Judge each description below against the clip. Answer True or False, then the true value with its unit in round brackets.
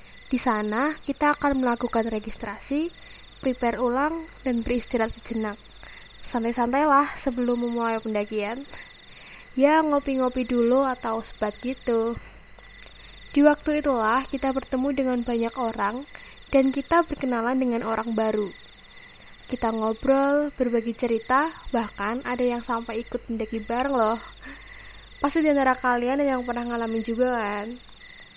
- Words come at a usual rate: True (120 wpm)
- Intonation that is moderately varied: True (3.0 semitones)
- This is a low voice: False (245 Hz)